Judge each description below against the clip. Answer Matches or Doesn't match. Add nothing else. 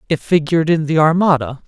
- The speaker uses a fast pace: Doesn't match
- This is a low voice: Doesn't match